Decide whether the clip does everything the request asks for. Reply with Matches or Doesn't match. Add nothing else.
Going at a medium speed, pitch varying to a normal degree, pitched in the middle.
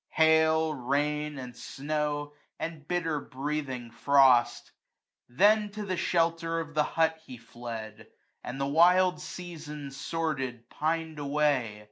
Doesn't match